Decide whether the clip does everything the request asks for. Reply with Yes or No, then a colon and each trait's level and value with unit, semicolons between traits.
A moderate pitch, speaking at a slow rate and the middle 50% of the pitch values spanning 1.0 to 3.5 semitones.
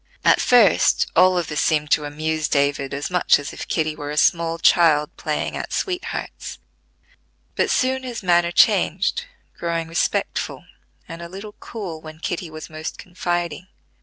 No: medium, 165 Hz; average, 155 wpm; average, 2.9 semitones